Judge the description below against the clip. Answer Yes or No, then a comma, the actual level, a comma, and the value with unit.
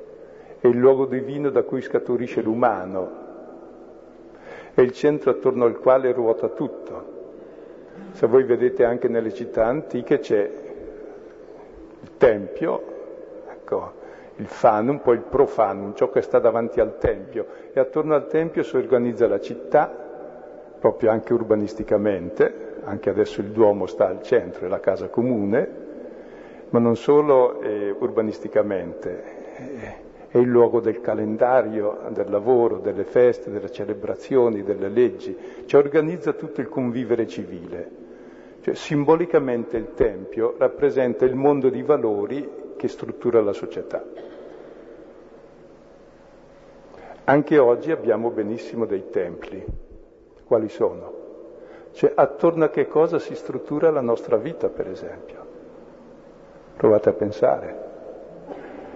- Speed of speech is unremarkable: Yes, average, 125 wpm